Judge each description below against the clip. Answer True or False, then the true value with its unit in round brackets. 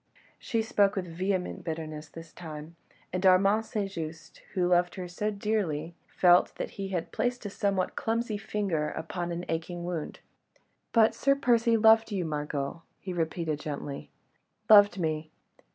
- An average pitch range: True (4.3 semitones)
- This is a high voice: False (180 Hz)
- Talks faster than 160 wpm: False (150 wpm)